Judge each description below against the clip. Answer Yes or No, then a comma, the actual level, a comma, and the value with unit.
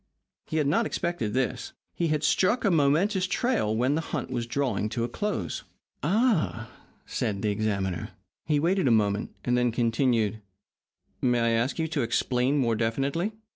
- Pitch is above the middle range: No, low, 130 Hz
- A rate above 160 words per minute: Yes, average, 170 wpm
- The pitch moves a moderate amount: No, wide, 6.3 semitones